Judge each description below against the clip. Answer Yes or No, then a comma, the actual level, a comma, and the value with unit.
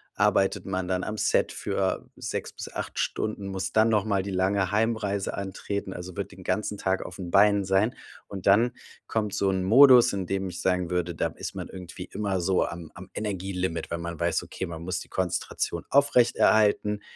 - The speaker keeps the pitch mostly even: Yes, narrow, 2.2 semitones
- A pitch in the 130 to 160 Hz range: No, very low, 95 Hz